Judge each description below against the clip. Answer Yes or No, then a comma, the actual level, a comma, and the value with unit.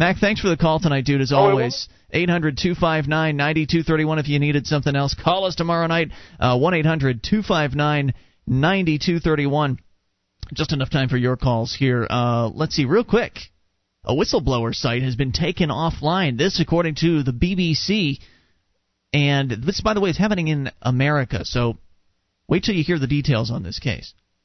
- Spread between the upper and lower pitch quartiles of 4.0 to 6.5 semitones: Yes, average, 4.9 semitones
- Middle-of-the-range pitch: Yes, medium, 145 Hz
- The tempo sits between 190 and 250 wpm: Yes, average, 200 wpm